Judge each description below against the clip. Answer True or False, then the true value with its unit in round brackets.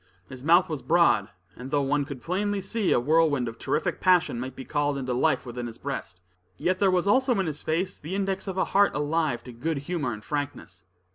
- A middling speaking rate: False (220 wpm)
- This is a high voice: False (150 Hz)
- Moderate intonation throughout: False (6.3 semitones)